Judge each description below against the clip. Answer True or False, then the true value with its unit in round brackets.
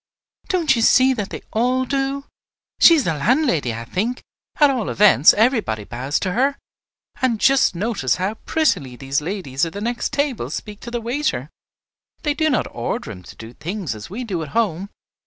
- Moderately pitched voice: False (215 Hz)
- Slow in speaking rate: False (190 wpm)